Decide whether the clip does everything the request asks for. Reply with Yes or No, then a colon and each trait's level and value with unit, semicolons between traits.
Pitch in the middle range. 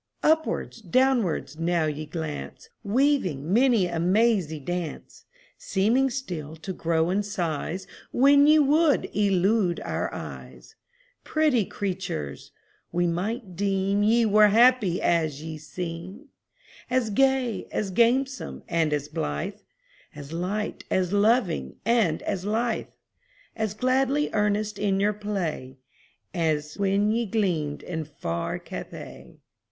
No: high, 195 Hz